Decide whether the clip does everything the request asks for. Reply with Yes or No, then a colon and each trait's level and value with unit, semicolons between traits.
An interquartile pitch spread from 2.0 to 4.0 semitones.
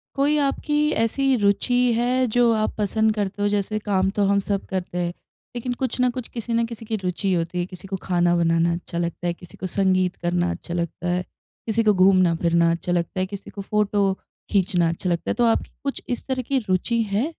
No: average, 4.5 semitones